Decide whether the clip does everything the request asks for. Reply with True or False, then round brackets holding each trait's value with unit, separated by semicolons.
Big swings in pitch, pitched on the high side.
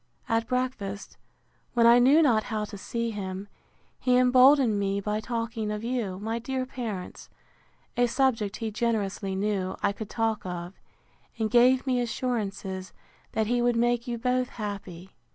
False (3.4 semitones; 225 Hz)